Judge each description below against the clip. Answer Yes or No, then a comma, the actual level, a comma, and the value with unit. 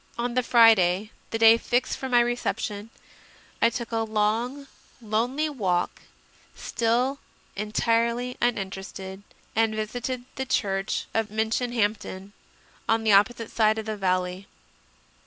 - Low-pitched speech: No, high, 225 Hz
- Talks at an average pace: No, slow, 120 wpm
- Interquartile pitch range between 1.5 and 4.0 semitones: Yes, average, 2.7 semitones